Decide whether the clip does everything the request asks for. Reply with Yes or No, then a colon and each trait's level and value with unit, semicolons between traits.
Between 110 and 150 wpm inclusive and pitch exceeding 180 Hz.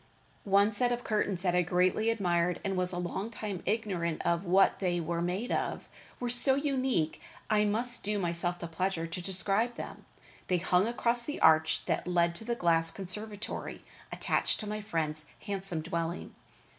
No: average, 175 wpm; high, 190 Hz